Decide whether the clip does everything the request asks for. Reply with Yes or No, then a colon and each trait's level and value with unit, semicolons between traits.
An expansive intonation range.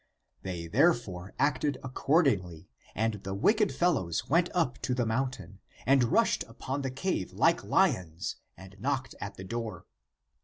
Yes: wide, 6.9 semitones